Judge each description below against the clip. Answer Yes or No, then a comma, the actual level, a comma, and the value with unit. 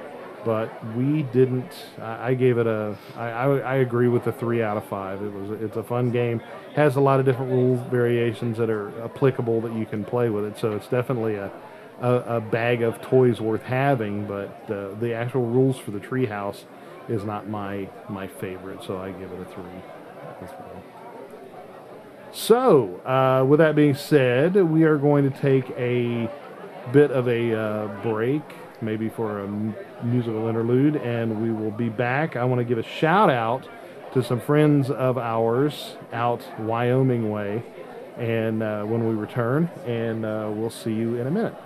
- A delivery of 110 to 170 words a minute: No, average, 180 wpm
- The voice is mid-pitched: No, low, 120 Hz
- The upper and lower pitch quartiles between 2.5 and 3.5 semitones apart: Yes, average, 2.9 semitones